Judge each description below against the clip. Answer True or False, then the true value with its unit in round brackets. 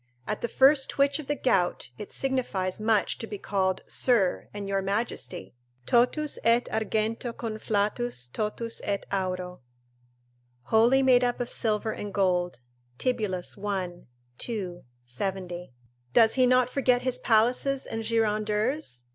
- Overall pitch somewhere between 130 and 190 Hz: False (220 Hz)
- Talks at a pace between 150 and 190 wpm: False (135 wpm)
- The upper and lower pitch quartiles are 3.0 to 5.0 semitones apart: True (4.2 semitones)